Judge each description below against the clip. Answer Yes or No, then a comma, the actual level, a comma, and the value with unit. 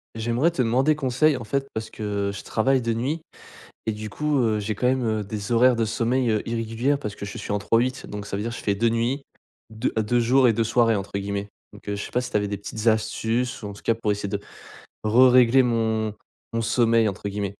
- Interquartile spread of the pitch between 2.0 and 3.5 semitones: Yes, average, 2.9 semitones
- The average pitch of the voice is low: Yes, low, 115 Hz